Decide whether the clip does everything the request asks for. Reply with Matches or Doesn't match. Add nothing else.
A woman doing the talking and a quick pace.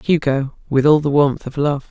Matches